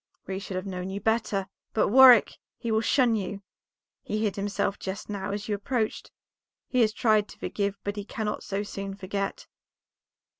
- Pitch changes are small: Yes, narrow, 1.7 semitones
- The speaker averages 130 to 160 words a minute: No, average, 180 wpm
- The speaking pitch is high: Yes, high, 205 Hz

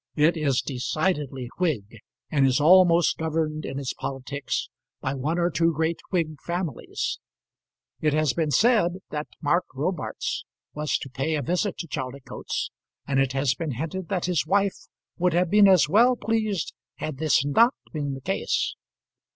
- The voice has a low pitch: No, medium, 155 Hz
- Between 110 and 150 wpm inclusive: No, average, 165 wpm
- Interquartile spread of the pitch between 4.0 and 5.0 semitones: Yes, average, 4.4 semitones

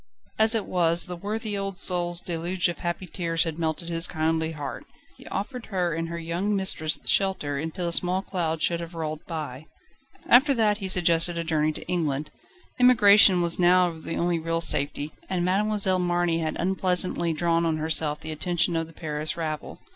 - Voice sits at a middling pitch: Yes, medium, 170 Hz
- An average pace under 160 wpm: No, average, 185 wpm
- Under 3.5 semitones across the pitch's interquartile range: Yes, narrow, 2.4 semitones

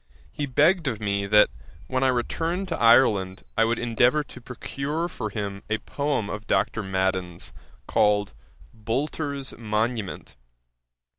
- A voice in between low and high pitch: No, low, 115 Hz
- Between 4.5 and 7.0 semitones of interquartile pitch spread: Yes, average, 5.0 semitones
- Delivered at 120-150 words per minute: Yes, slow, 135 wpm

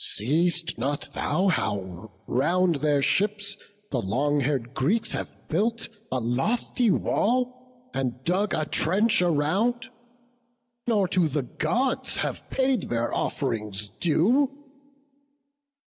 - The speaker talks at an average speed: No, slow, 115 wpm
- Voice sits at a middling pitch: Yes, medium, 165 Hz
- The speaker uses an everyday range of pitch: No, wide, 8.7 semitones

